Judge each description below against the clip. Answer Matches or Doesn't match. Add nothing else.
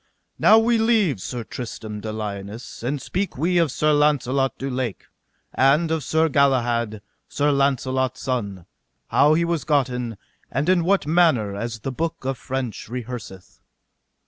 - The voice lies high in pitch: Doesn't match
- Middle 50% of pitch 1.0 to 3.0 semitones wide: Doesn't match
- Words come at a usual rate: Matches